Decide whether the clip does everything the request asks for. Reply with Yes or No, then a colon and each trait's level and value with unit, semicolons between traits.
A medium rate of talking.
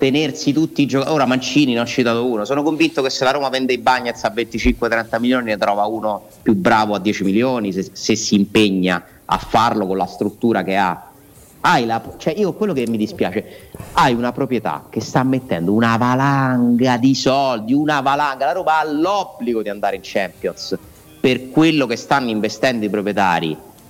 No: fast, 190 wpm